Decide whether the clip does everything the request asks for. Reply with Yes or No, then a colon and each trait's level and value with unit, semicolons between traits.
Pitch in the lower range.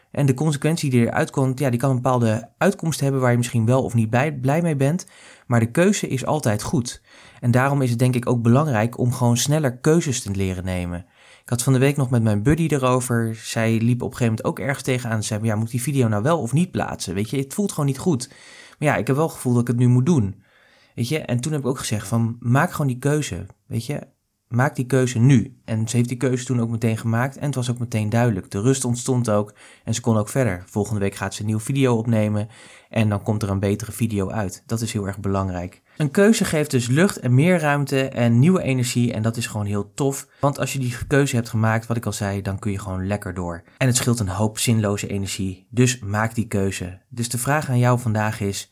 Yes: low, 120 Hz